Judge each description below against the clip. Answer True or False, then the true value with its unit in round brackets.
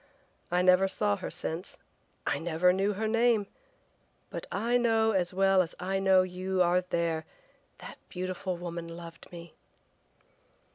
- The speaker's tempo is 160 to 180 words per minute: False (145 wpm)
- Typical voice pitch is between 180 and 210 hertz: True (185 Hz)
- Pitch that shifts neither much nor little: False (2.0 semitones)